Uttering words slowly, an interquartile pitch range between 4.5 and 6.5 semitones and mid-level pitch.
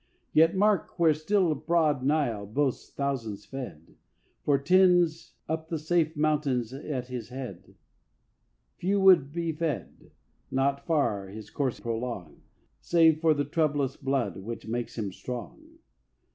Yes: slow, 130 wpm; average, 4.8 semitones; medium, 145 Hz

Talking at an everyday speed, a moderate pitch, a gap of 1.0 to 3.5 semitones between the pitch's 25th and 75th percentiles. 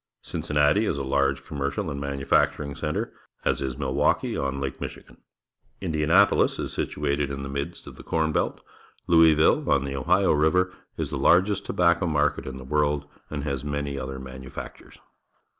No: average, 165 wpm; very low, 70 Hz; narrow, 2.5 semitones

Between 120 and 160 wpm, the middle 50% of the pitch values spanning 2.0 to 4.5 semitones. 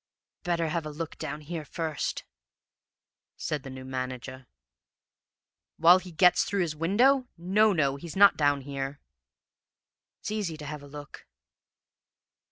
Yes: average, 140 wpm; average, 4.0 semitones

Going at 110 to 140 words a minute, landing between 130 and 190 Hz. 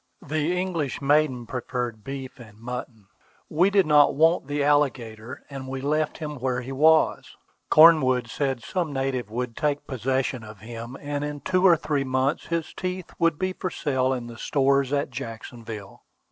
No: average, 170 wpm; low, 135 Hz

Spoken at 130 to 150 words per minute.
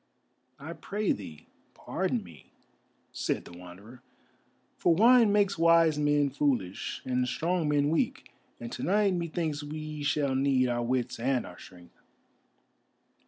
Yes: slow, 135 wpm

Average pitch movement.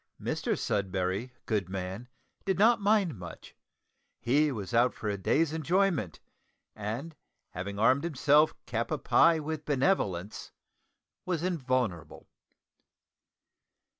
No: wide, 8.1 semitones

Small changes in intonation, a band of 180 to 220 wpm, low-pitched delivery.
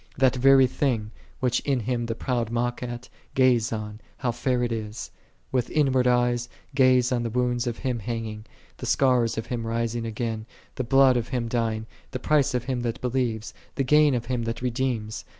Yes: narrow, 2.0 semitones; average, 190 wpm; low, 120 Hz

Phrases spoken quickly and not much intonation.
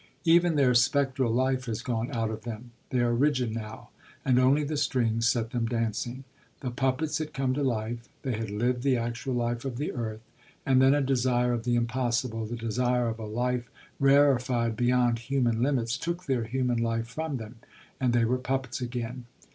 No: average, 190 wpm; narrow, 2.3 semitones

